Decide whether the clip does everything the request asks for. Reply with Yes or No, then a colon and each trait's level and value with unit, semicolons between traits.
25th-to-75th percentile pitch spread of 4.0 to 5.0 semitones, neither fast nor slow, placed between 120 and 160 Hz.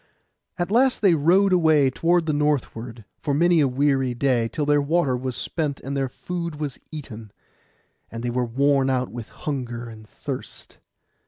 Yes: average, 4.3 semitones; average, 165 wpm; medium, 140 Hz